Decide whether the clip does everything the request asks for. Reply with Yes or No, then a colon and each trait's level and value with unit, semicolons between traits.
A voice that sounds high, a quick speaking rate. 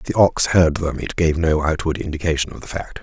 No: very low, 80 Hz; fast, 260 wpm